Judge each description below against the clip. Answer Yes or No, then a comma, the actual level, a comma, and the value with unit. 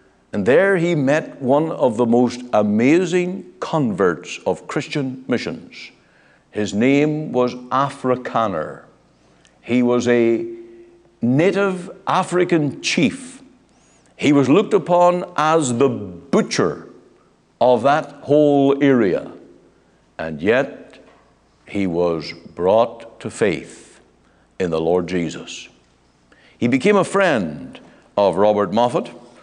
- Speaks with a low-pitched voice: Yes, low, 130 Hz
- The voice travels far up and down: Yes, wide, 7.3 semitones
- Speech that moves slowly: Yes, slow, 105 wpm